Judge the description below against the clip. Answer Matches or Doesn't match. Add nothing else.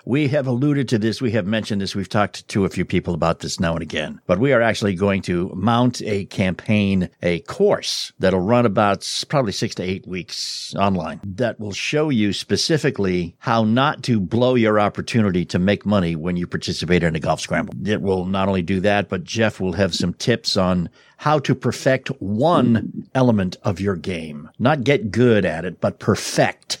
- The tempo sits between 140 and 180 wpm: Doesn't match